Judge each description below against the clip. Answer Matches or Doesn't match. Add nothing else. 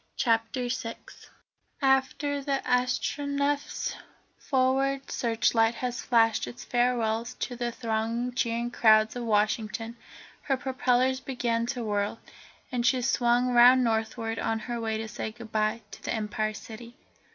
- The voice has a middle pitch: Doesn't match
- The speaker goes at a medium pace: Doesn't match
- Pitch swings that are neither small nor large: Doesn't match